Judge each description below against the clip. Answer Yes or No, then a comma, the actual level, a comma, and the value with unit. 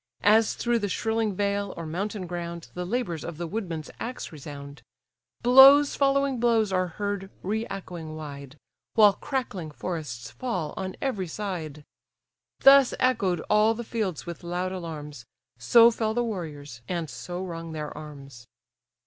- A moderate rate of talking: Yes, average, 150 wpm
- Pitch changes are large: Yes, wide, 5.9 semitones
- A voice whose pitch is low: No, medium, 185 Hz